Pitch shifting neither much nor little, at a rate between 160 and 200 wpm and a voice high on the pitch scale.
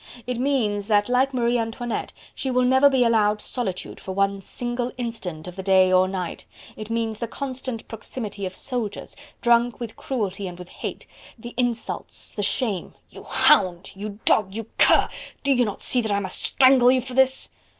Yes: average, 3.9 semitones; average, 185 wpm; high, 225 Hz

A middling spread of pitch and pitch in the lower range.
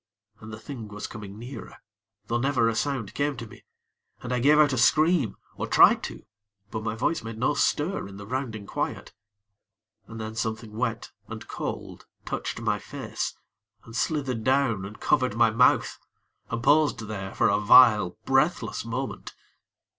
Yes: average, 3.7 semitones; low, 115 Hz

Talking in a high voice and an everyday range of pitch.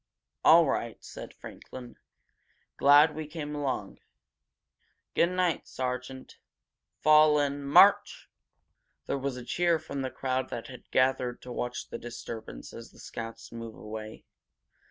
No: low, 130 Hz; average, 3.7 semitones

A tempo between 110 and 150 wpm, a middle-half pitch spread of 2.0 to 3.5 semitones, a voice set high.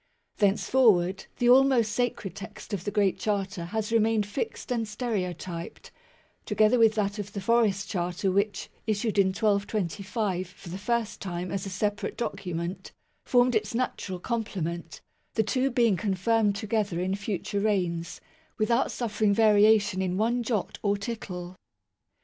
Yes: average, 145 wpm; average, 3.0 semitones; high, 205 Hz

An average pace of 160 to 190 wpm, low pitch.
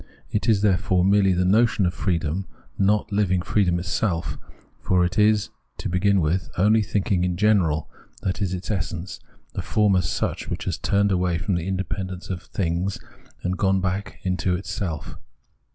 Yes: average, 170 wpm; very low, 95 Hz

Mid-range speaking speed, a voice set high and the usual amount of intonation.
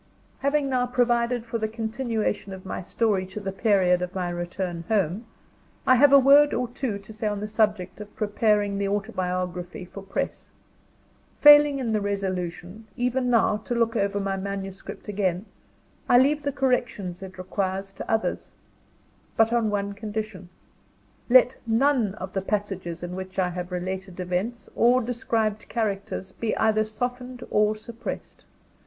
Yes: average, 160 wpm; high, 210 Hz; average, 3.8 semitones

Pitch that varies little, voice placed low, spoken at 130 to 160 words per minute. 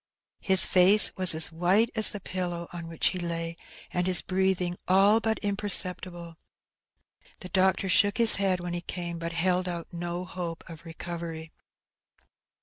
No: narrow, 2.0 semitones; medium, 180 Hz; average, 155 wpm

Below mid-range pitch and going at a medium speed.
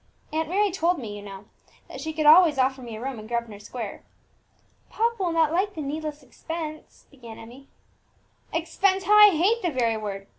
No: very high, 300 Hz; average, 190 wpm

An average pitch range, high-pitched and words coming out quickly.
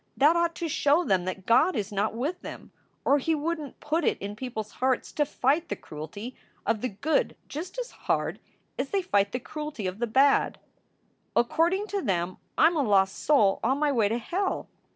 No: wide, 7.2 semitones; very high, 265 Hz; fast, 210 wpm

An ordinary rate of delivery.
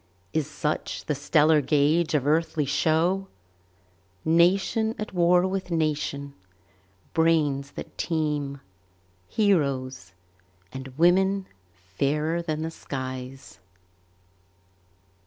No: slow, 90 wpm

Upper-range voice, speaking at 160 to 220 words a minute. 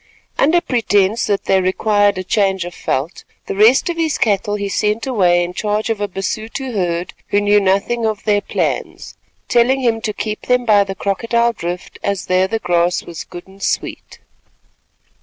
Yes: high, 205 Hz; average, 180 wpm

